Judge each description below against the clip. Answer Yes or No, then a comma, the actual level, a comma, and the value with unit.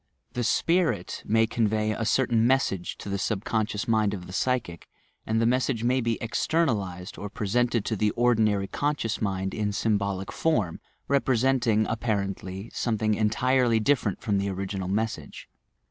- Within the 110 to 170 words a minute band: Yes, average, 155 wpm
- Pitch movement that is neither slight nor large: Yes, average, 3.3 semitones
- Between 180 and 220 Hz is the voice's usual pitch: No, low, 110 Hz